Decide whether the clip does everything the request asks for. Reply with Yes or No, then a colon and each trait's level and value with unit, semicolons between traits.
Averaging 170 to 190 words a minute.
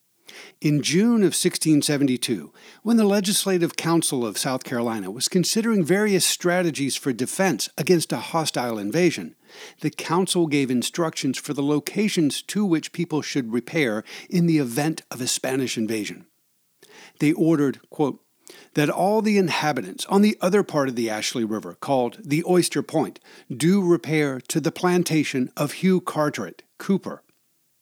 No: average, 150 wpm